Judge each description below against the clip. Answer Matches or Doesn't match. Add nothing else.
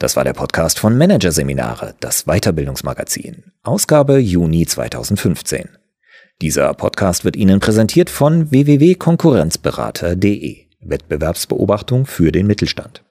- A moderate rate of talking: Doesn't match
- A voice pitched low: Matches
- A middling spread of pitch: Doesn't match